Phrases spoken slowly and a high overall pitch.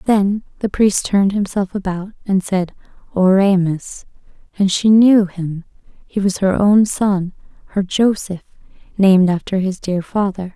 Yes: slow, 130 wpm; high, 195 Hz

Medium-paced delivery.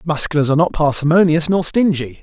Yes: average, 160 wpm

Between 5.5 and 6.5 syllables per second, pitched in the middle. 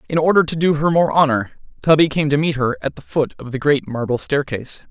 Yes: 5.9 syllables/s; medium, 145 Hz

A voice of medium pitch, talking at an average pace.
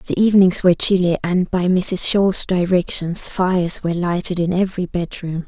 Yes: medium, 180 Hz; average, 165 wpm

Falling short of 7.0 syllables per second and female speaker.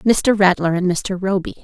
Yes: 4.6 syllables/s; female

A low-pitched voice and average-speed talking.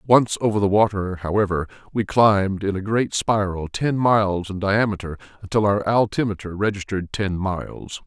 Yes: low, 100 Hz; average, 155 wpm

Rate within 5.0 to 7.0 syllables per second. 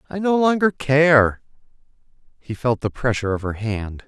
No: 4.8 syllables/s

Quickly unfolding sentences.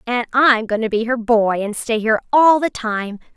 Yes: fast, 230 wpm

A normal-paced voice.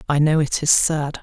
No: fast, 245 wpm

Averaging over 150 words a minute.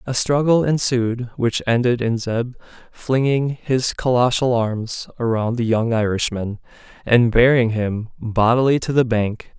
No: average, 140 wpm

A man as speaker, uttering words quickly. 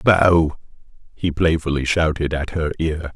No: male; slow, 135 wpm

